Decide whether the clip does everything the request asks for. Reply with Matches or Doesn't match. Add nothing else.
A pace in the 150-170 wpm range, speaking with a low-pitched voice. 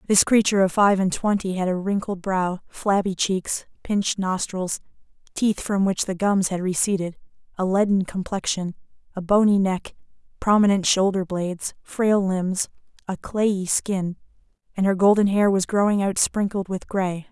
Doesn't match